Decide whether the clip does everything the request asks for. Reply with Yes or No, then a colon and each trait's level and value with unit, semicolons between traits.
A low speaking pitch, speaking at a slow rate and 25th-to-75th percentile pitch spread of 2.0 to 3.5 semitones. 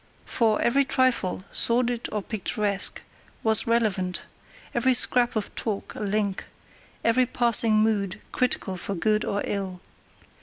No: high, 215 Hz; slow, 125 wpm; average, 3.0 semitones